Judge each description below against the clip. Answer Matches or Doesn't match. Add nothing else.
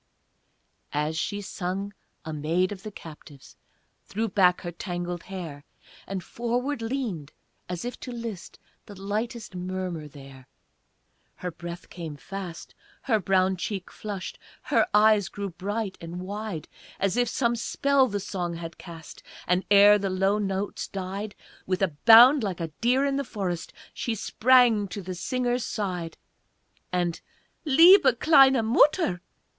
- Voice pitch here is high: Matches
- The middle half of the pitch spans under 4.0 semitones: Doesn't match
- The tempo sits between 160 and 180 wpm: Doesn't match